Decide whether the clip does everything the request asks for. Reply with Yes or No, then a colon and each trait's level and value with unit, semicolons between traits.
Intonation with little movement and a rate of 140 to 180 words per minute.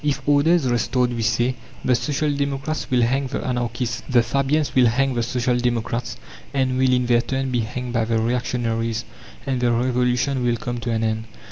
No: narrow, 2.1 semitones; average, 200 wpm